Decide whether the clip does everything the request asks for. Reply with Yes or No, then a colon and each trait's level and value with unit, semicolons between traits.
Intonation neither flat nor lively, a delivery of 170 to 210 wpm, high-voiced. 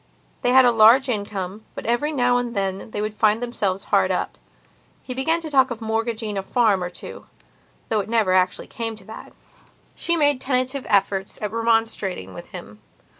Yes: average, 3.6 semitones; average, 185 wpm; high, 225 Hz